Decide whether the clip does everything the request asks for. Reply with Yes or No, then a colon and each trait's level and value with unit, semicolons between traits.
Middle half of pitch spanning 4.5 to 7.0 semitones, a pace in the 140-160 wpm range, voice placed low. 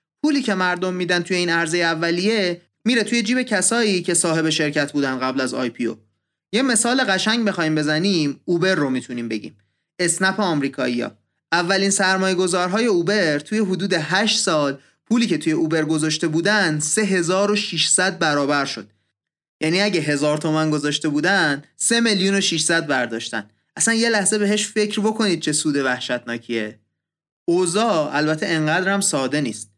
No: average, 5.2 semitones; average, 145 wpm; medium, 170 Hz